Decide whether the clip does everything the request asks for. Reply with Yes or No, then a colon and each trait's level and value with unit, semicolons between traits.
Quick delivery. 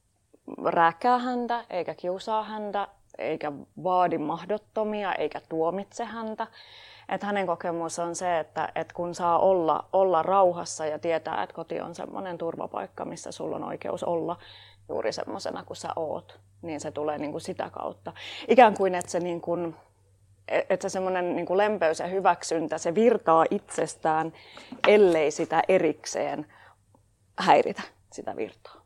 No: average, 135 wpm